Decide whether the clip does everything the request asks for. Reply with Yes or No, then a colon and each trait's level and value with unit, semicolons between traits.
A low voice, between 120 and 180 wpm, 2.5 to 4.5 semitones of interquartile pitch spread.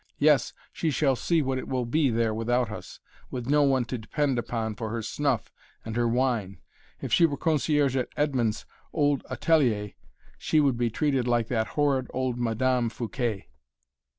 Yes: low, 125 Hz; average, 175 wpm; average, 3.6 semitones